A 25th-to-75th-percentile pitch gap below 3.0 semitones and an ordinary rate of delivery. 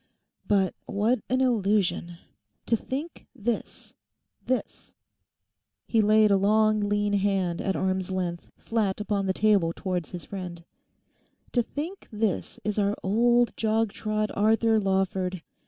No: narrow, 2.6 semitones; slow, 120 wpm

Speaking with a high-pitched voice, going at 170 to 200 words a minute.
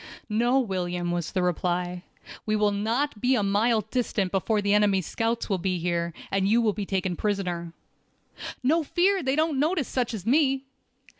Yes: high, 210 Hz; average, 175 wpm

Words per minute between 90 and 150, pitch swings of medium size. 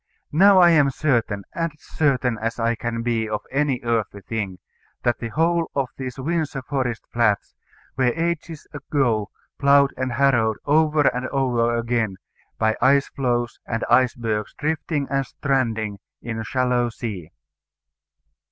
Yes: average, 145 wpm; average, 3.6 semitones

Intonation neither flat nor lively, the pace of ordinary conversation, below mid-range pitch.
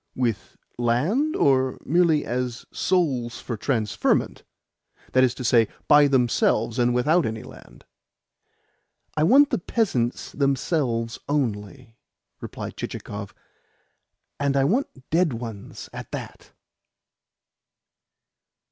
No: average, 4.6 semitones; slow, 105 wpm; low, 130 Hz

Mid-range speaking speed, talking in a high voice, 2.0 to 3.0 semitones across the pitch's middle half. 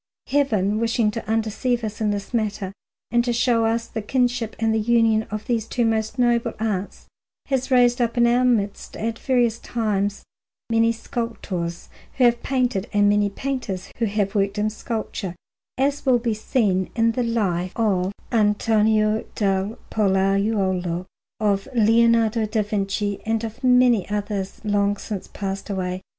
Yes: average, 155 wpm; high, 220 Hz; narrow, 2.6 semitones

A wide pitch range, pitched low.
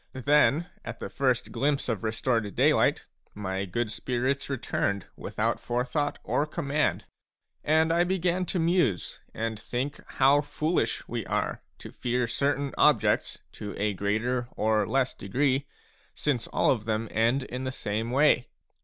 No: average, 4.4 semitones; low, 125 Hz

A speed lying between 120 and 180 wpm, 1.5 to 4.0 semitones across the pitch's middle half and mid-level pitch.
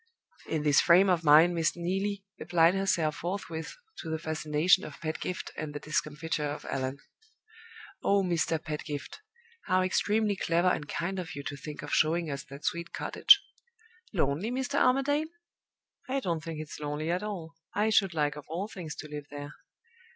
Yes: average, 170 wpm; average, 3.7 semitones; medium, 165 Hz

